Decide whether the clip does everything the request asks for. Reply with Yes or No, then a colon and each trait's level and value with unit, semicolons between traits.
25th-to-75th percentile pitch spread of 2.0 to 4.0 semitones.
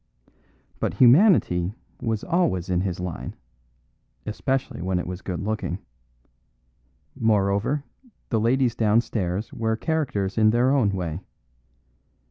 No: average, 4.6 semitones